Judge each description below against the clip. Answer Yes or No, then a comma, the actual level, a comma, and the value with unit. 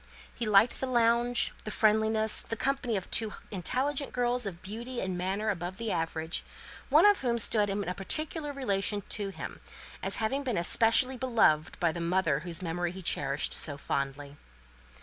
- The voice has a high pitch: Yes, high, 210 Hz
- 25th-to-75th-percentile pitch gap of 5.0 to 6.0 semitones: Yes, average, 5.3 semitones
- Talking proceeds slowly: No, average, 170 wpm